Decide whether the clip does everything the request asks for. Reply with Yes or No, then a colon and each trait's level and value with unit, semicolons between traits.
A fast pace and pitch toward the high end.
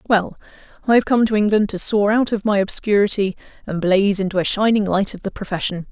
Yes: fast, 215 wpm; high, 205 Hz